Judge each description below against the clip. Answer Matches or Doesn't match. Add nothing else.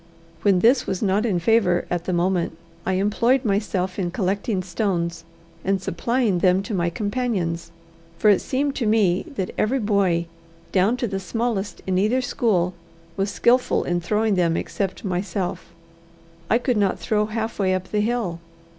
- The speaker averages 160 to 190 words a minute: Matches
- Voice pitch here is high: Matches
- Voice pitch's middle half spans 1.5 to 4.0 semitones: Matches